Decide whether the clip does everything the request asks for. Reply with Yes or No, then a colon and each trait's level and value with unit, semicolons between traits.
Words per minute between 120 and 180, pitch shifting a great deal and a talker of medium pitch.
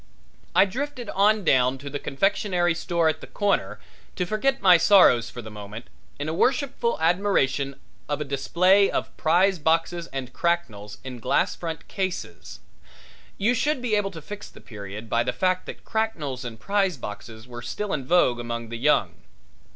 Yes: average, 175 wpm; wide, 7.8 semitones; medium, 165 Hz